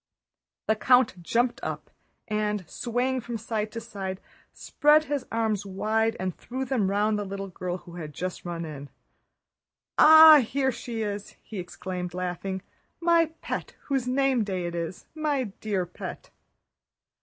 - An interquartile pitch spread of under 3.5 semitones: No, average, 5.3 semitones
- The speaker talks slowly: No, average, 145 wpm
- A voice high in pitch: Yes, high, 215 Hz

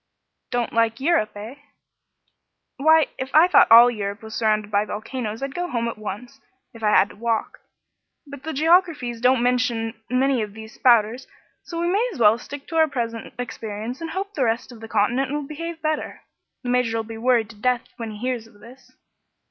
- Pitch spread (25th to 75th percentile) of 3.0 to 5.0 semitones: Yes, average, 3.7 semitones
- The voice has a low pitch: No, high, 245 Hz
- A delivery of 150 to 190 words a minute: No, average, 200 wpm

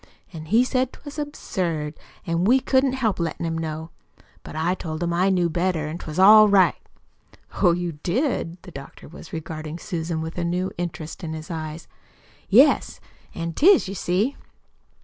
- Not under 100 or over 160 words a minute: No, average, 170 wpm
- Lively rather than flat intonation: No, average, 3.7 semitones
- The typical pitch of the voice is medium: Yes, medium, 175 Hz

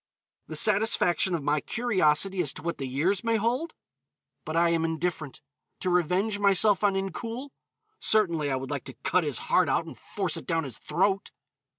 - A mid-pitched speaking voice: Yes, medium, 180 Hz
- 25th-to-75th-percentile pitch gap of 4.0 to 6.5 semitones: Yes, average, 4.7 semitones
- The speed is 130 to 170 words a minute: No, average, 185 wpm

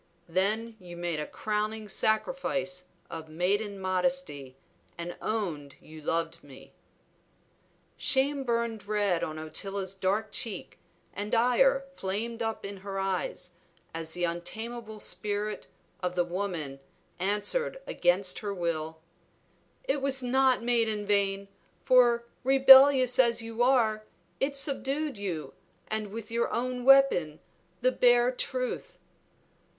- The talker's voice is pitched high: Yes, high, 210 Hz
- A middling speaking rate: No, slow, 125 wpm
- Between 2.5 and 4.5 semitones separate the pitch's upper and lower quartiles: No, average, 5.2 semitones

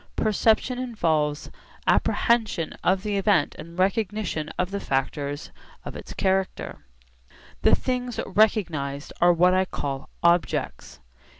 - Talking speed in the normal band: No, slow, 115 wpm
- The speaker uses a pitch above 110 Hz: Yes, medium, 185 Hz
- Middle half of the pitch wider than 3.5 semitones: Yes, wide, 5.5 semitones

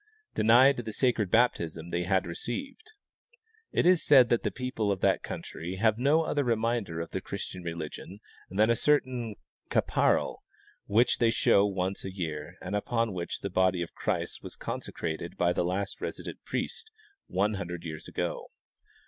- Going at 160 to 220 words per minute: Yes, average, 165 wpm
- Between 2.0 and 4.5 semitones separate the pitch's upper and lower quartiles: No, average, 5.3 semitones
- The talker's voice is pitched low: Yes, low, 100 Hz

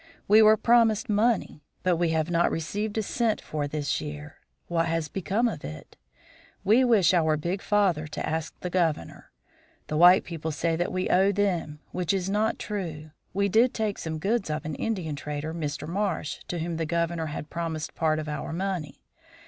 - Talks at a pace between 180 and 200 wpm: Yes, average, 190 wpm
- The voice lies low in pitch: No, medium, 170 Hz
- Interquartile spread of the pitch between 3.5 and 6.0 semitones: Yes, average, 4.5 semitones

